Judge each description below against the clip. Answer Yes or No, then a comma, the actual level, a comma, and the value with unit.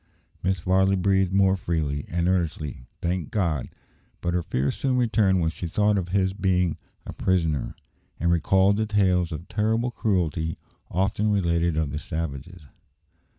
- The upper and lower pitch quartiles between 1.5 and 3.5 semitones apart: Yes, average, 3.0 semitones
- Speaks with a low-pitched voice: Yes, very low, 90 Hz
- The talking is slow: No, average, 150 wpm